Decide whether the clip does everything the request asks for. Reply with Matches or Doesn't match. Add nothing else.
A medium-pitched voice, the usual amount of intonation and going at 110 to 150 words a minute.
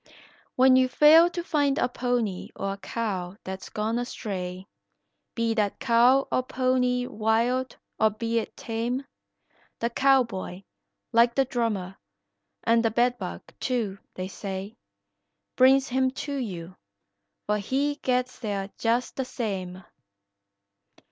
Doesn't match